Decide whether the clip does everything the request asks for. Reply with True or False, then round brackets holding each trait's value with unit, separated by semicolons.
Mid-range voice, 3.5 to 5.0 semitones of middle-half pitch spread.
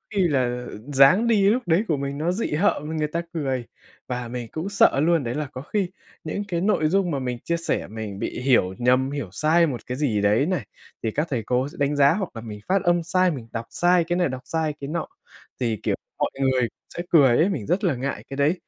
False (145 Hz; 5.5 semitones)